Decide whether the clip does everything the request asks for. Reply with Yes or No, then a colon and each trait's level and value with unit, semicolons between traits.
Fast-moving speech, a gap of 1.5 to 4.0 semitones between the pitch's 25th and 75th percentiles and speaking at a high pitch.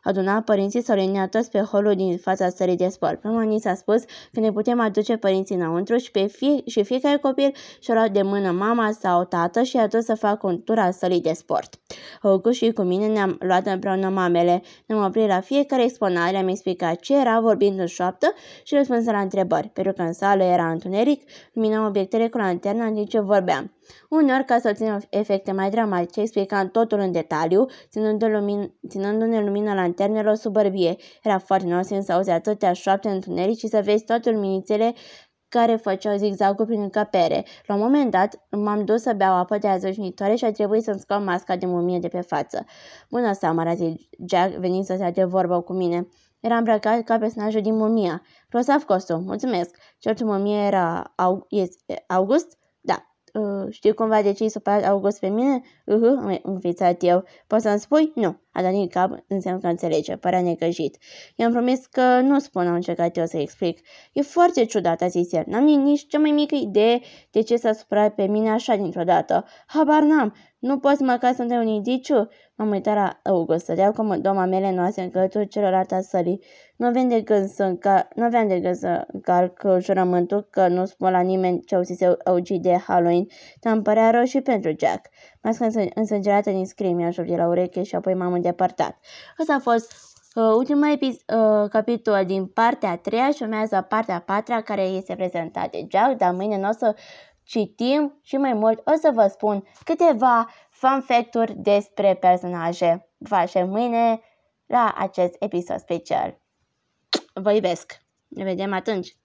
Yes: fast, 185 wpm; average, 3.6 semitones; high, 205 Hz